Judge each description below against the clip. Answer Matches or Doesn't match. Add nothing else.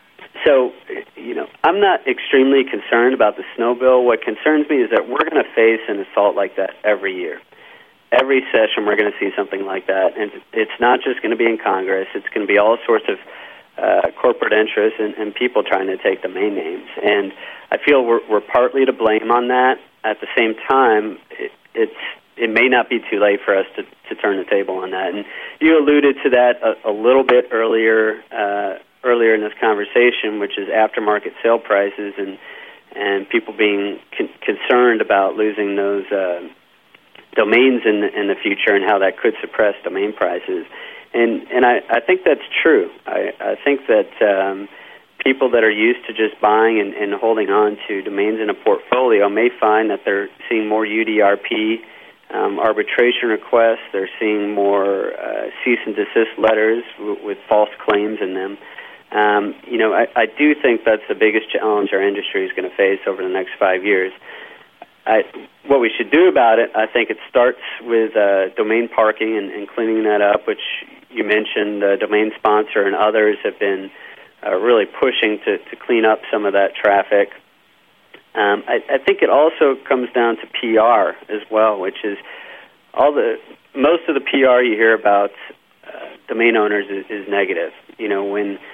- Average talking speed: Matches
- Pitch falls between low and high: Doesn't match